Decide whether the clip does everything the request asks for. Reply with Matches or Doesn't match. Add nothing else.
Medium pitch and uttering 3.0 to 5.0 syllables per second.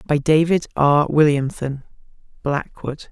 Matches